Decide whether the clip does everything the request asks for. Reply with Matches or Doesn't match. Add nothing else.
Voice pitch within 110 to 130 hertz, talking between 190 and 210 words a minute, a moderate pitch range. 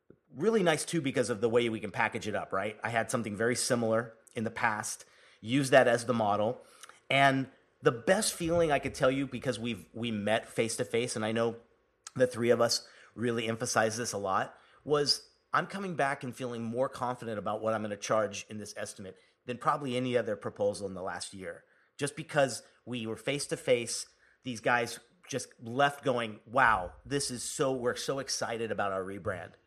Matches